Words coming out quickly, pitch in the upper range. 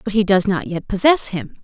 Yes: fast, 255 wpm; high, 200 Hz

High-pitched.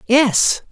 Yes: high, 235 Hz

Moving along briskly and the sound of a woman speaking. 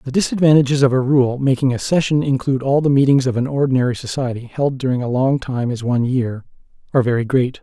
No: fast, 210 wpm; male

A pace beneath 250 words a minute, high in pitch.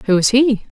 Yes: fast, 225 wpm; high, 230 Hz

